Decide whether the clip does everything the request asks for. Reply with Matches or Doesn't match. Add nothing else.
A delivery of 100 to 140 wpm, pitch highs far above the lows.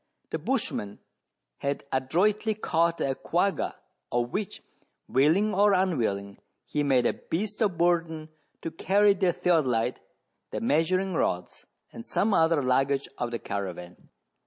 Matches